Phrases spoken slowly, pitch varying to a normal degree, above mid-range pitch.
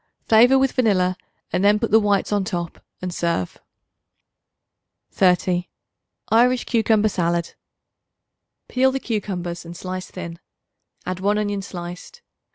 Yes: slow, 125 wpm; average, 3.8 semitones; high, 195 Hz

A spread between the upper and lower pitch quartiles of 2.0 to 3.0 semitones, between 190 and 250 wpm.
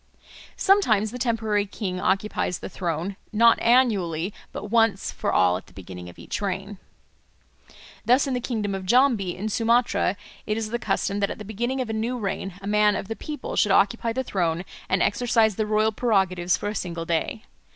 No: average, 3.6 semitones; average, 195 wpm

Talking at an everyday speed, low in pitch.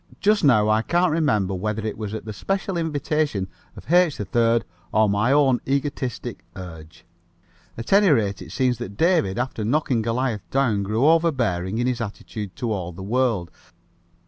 Yes: average, 170 wpm; low, 115 Hz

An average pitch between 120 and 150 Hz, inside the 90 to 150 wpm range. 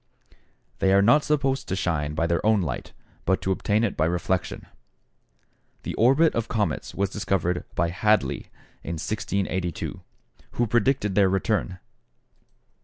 No: low, 100 Hz; average, 140 wpm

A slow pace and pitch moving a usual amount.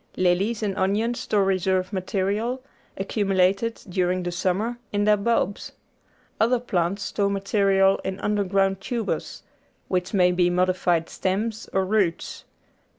No: slow, 125 wpm; narrow, 2.2 semitones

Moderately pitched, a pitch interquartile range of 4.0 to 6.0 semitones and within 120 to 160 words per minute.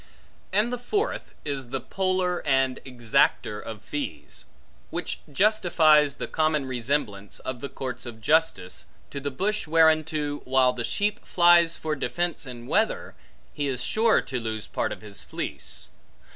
Yes: medium, 145 Hz; wide, 5.4 semitones; average, 150 wpm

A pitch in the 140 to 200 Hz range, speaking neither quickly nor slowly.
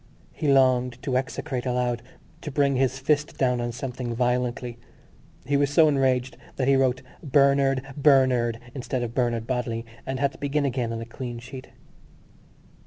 No: low, 130 Hz; average, 165 wpm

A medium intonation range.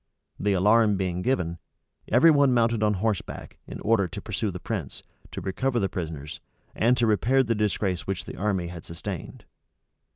Yes: average, 4.3 semitones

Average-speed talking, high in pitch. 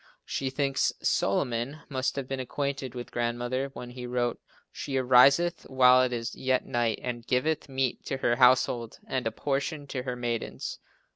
No: average, 165 wpm; low, 130 Hz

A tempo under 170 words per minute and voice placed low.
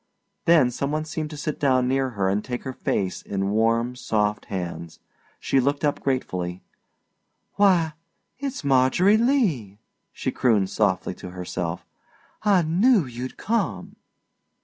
Yes: average, 140 wpm; low, 130 Hz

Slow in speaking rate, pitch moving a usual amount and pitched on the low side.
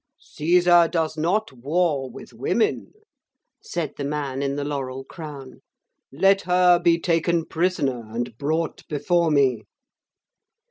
No: slow, 125 wpm; average, 4.0 semitones; medium, 155 Hz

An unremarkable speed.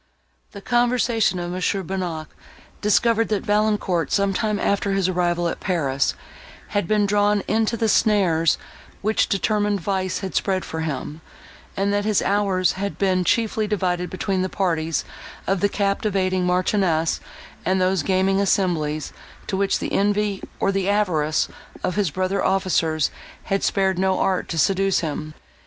Yes: average, 150 wpm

